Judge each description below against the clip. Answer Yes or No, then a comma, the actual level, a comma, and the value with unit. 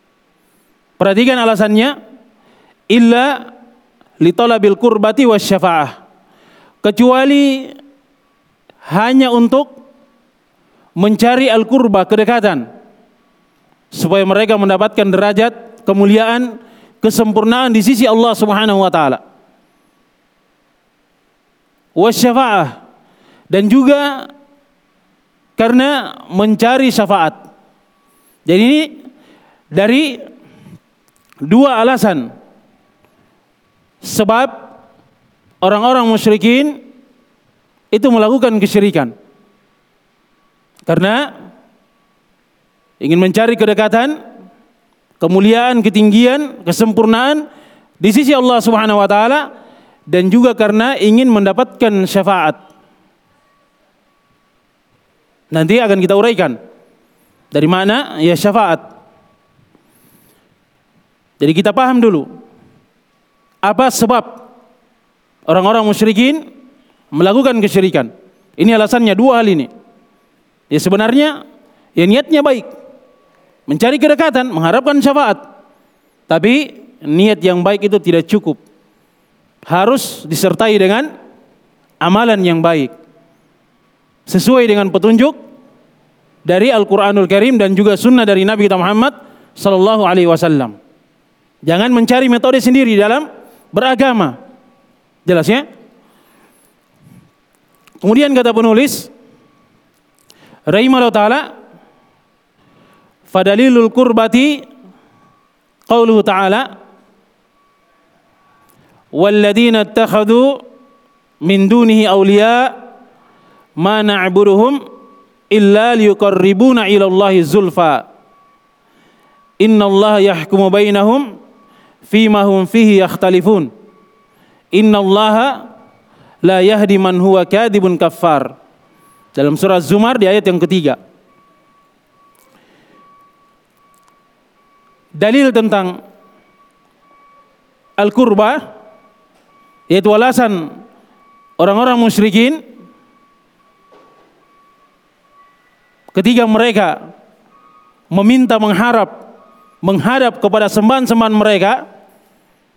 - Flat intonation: No, average, 4.4 semitones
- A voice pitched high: Yes, high, 225 Hz